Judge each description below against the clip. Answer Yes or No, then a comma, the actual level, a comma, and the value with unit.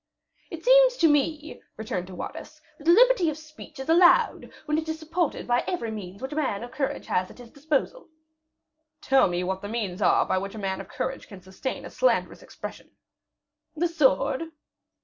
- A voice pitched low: No, very high, 275 Hz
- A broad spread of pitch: Yes, wide, 8.1 semitones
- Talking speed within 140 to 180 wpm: No, average, 190 wpm